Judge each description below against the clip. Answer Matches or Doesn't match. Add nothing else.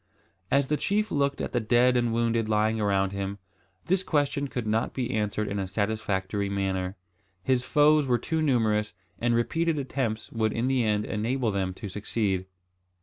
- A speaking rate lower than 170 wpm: Doesn't match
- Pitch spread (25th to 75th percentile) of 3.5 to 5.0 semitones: Matches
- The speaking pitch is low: Matches